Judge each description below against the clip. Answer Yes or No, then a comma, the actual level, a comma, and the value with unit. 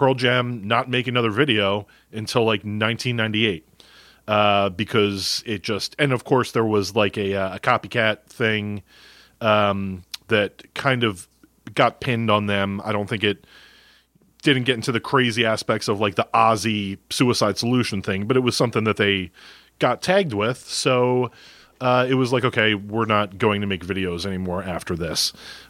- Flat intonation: No, average, 3.3 semitones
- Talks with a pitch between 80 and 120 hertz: Yes, low, 110 Hz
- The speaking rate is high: No, average, 170 wpm